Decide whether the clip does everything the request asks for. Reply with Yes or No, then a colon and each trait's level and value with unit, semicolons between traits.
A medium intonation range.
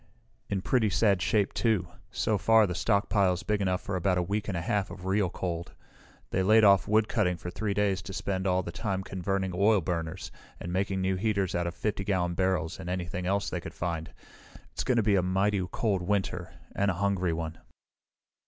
No: narrow, 2.2 semitones